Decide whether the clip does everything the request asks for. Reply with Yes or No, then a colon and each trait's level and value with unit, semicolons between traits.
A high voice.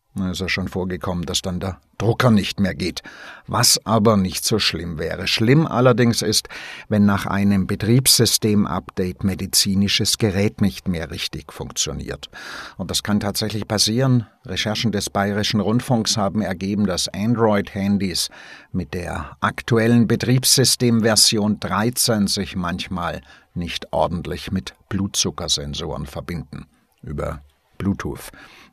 No: low, 100 Hz